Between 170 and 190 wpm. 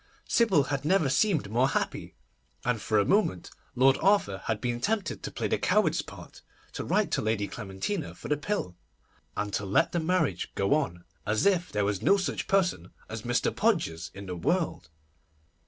Yes: average, 185 wpm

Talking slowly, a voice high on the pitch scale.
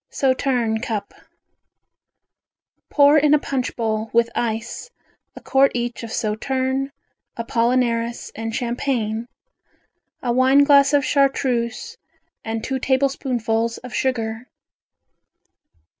Yes: slow, 100 wpm; high, 245 Hz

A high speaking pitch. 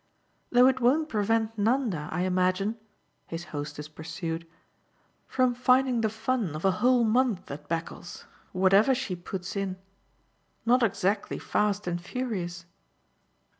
Yes: high, 200 Hz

